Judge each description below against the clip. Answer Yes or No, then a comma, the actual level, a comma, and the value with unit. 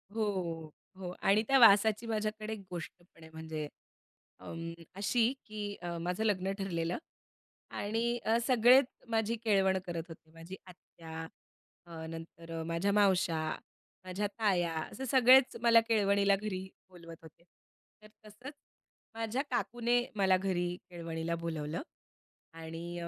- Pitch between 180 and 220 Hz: Yes, high, 190 Hz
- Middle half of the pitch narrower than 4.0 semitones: No, average, 4.6 semitones